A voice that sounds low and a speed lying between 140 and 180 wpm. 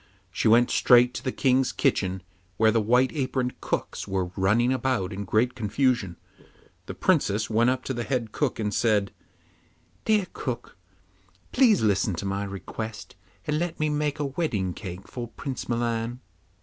Yes: low, 120 Hz; average, 160 wpm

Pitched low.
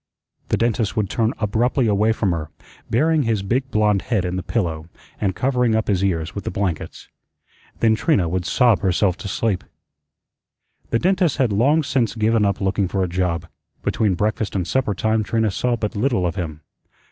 Yes: low, 105 Hz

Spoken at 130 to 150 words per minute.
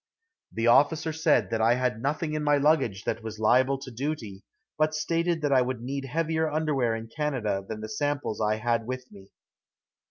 No: average, 190 wpm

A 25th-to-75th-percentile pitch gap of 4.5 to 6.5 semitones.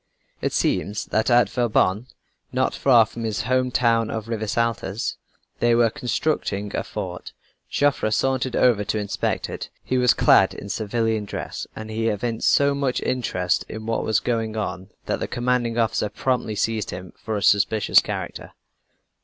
No: narrow, 2.4 semitones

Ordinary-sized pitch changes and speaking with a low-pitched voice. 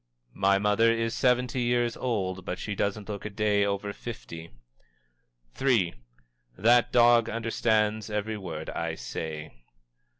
Yes: average, 3.0 semitones; low, 105 Hz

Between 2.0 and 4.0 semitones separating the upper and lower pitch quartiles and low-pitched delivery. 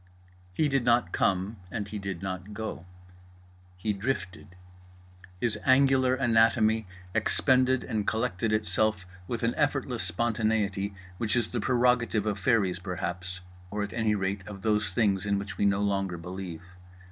Yes: average, 3.4 semitones; low, 105 Hz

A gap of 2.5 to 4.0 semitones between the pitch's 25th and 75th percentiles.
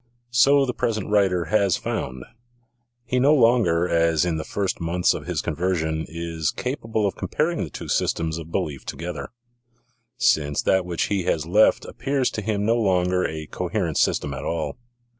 No: average, 5.2 semitones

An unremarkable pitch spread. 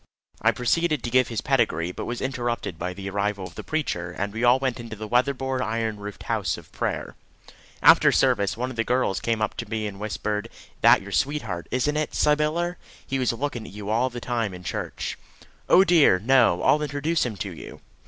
Yes: average, 4.5 semitones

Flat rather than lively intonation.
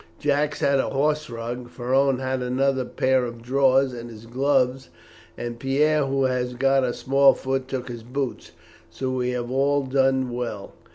Yes: narrow, 1.7 semitones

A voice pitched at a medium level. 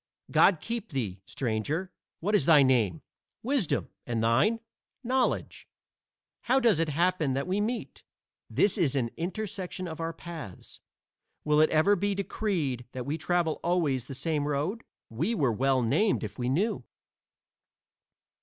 Yes: medium, 160 Hz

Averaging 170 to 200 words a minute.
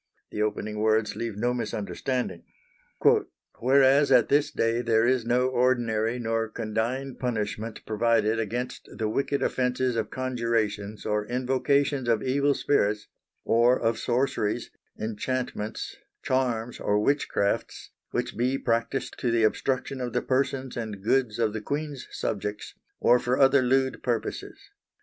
No: slow, 135 wpm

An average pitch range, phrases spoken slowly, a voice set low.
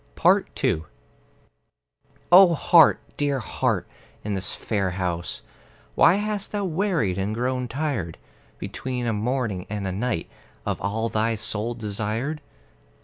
No: wide, 6.4 semitones; slow, 125 wpm; low, 115 Hz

